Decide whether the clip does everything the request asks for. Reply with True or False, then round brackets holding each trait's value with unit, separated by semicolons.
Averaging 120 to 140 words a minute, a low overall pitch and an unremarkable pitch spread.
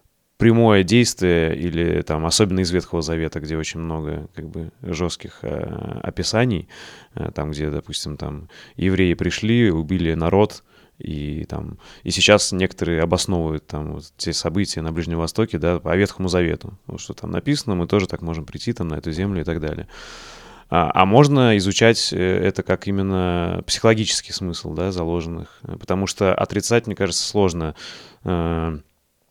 False (155 wpm; 90 Hz; 3.3 semitones)